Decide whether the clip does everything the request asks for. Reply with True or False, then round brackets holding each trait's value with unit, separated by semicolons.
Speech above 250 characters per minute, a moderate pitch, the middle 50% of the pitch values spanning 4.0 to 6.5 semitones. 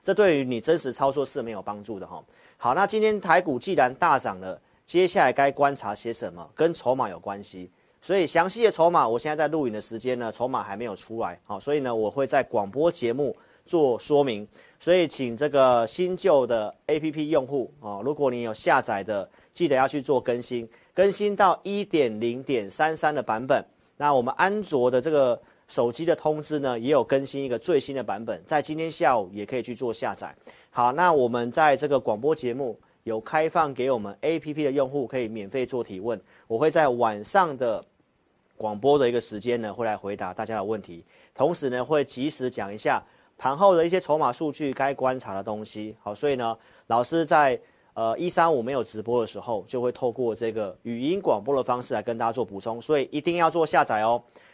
False (310 characters per minute; 130 Hz; 5.2 semitones)